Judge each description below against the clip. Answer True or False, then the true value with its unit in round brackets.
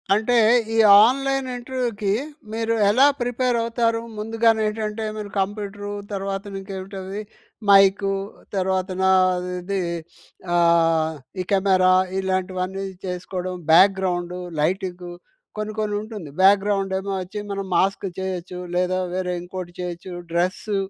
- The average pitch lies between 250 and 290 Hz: False (195 Hz)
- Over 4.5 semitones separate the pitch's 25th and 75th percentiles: False (2.4 semitones)